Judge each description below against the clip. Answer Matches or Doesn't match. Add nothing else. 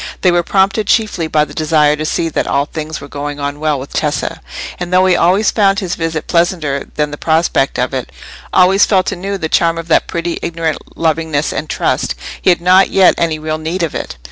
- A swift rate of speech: Matches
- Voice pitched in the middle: Matches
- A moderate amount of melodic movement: Matches